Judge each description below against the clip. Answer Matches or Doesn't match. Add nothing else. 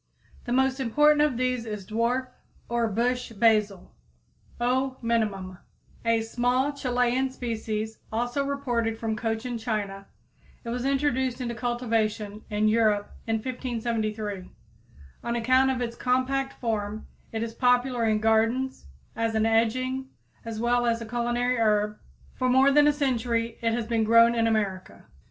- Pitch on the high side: Matches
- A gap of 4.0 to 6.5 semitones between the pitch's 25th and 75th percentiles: Doesn't match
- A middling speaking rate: Matches